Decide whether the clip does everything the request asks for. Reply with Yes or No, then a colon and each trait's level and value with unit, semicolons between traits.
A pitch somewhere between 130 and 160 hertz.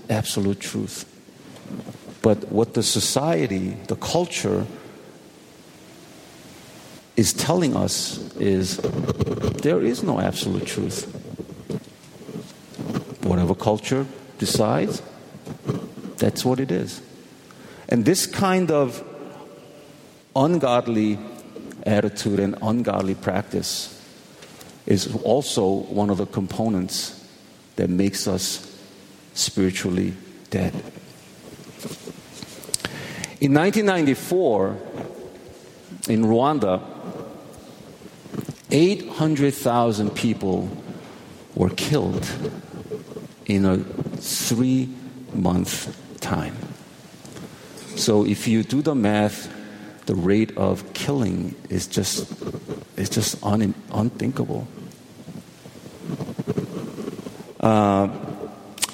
No: low, 110 Hz